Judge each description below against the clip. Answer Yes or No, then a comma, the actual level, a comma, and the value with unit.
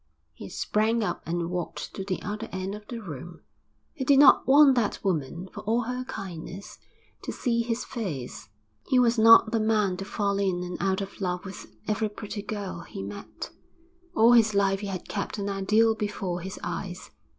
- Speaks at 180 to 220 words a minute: Yes, average, 190 wpm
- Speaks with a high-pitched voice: Yes, high, 200 Hz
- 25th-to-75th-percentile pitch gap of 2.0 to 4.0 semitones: Yes, average, 3.4 semitones